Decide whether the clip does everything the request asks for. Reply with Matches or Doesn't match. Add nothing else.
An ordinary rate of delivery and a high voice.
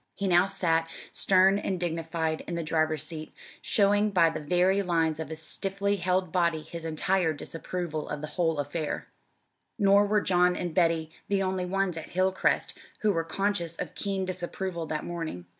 Doesn't match